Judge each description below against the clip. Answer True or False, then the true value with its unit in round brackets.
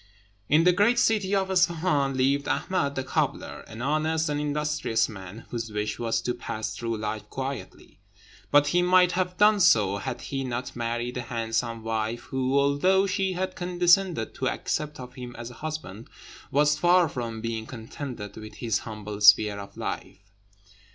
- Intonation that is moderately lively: False (7.1 semitones)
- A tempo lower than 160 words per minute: False (170 wpm)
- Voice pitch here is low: True (130 Hz)